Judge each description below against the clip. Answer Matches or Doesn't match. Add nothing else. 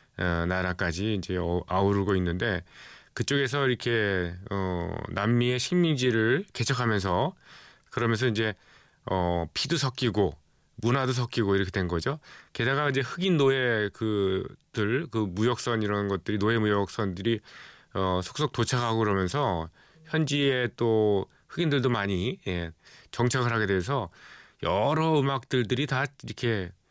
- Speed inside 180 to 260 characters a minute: Doesn't match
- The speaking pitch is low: Matches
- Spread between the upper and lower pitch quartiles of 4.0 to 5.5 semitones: Matches